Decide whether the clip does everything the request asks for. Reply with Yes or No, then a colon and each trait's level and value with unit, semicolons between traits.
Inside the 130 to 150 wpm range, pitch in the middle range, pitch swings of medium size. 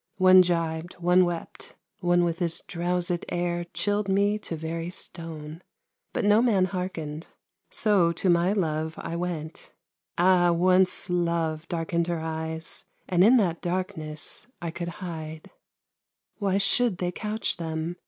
No: average, 140 wpm; medium, 175 Hz; narrow, 2.1 semitones